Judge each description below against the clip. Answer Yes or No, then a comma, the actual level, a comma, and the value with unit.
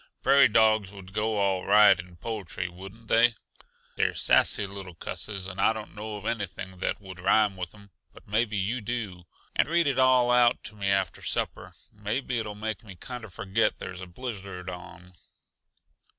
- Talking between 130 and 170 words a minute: No, average, 180 wpm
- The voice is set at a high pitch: No, low, 105 Hz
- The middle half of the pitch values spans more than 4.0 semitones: No, average, 3.0 semitones